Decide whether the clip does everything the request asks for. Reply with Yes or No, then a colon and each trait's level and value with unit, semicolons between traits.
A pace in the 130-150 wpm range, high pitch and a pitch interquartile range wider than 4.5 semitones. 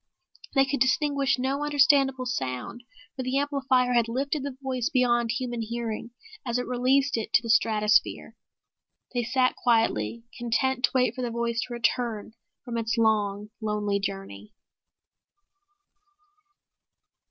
No: slow, 135 wpm; high, 245 Hz; average, 2.7 semitones